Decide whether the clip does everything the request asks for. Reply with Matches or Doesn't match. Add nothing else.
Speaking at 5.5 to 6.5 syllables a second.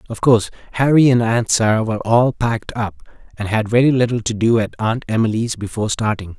Matches